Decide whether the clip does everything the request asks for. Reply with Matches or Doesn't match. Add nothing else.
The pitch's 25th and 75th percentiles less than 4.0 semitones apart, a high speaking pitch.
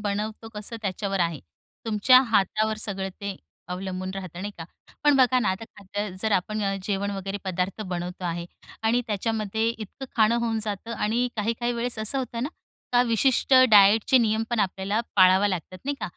Matches